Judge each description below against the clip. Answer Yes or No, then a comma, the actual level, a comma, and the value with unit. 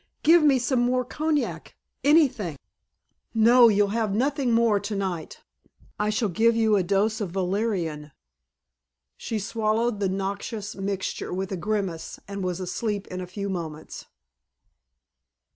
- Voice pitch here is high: Yes, high, 210 Hz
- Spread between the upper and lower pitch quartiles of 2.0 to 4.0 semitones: Yes, average, 3.4 semitones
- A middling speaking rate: No, slow, 130 wpm